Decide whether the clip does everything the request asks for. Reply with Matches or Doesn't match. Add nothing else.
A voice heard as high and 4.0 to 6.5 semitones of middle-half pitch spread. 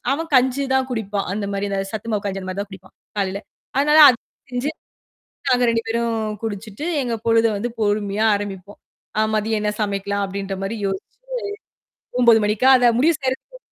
Doesn't match